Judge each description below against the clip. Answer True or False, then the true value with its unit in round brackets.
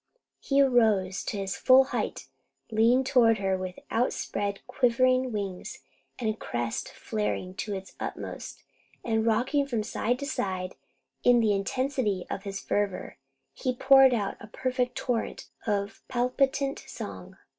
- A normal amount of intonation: True (4.3 semitones)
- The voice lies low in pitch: False (225 Hz)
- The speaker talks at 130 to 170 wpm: True (135 wpm)